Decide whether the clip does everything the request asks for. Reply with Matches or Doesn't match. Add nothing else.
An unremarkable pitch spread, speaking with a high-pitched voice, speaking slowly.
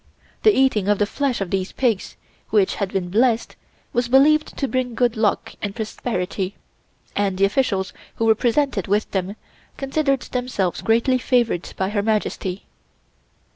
Doesn't match